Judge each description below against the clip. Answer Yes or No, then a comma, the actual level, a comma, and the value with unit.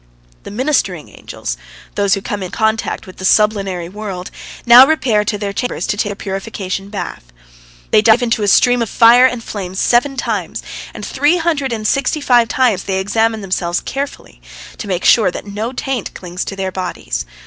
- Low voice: No, high, 215 Hz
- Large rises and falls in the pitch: No, average, 4.0 semitones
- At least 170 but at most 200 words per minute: Yes, average, 185 wpm